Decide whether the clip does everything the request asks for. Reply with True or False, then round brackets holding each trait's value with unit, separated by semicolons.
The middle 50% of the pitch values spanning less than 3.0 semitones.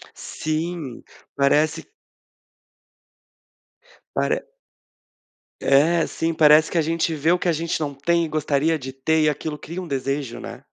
True (2.6 semitones)